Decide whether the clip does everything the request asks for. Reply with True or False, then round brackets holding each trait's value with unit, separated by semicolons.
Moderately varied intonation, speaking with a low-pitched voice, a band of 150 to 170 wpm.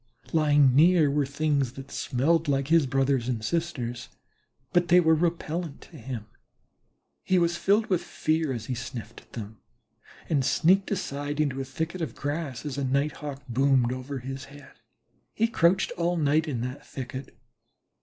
False (3.8 semitones; 145 Hz; 165 wpm)